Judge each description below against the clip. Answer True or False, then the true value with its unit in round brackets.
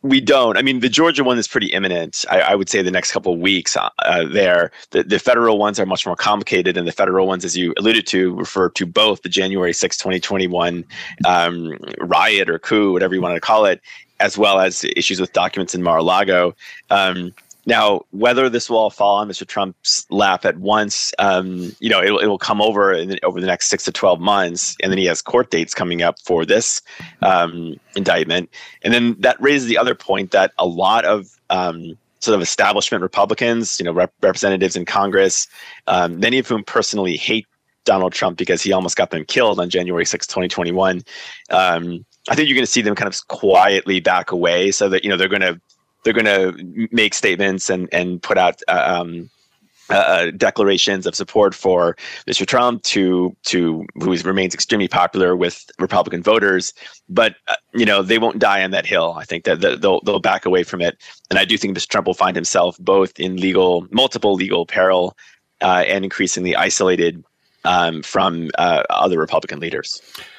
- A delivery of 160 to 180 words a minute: False (200 wpm)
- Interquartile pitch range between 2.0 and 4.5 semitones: True (3.4 semitones)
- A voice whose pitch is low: True (95 Hz)